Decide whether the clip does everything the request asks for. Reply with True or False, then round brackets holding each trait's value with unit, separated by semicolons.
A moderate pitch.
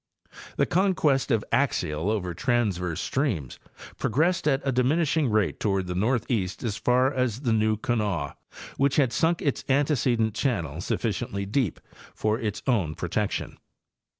False (115 Hz)